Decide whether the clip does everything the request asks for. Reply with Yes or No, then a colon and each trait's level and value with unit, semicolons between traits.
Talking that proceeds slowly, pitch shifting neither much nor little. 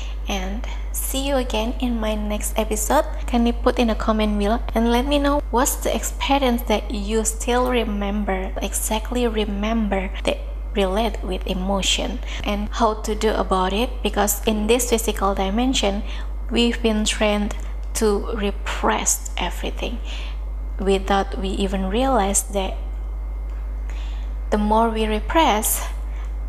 Yes: slow, 130 wpm; average, 3.2 semitones